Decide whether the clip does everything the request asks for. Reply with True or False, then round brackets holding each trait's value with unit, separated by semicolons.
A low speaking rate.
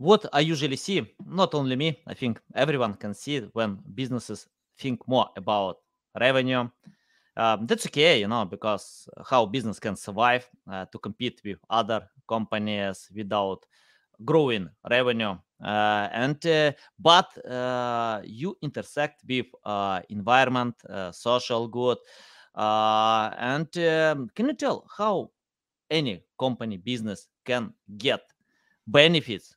True (130 wpm)